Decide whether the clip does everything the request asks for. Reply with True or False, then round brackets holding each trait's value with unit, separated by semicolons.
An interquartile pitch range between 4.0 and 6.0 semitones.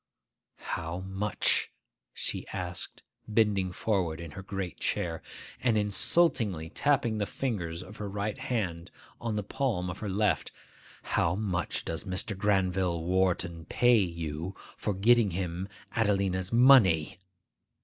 False (3.3 semitones)